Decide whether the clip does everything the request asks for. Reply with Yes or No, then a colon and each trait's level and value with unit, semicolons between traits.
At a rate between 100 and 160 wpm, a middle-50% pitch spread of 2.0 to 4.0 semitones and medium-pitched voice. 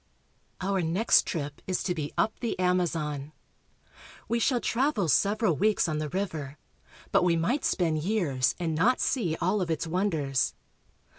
No: average, 155 wpm; average, 4.8 semitones; medium, 175 Hz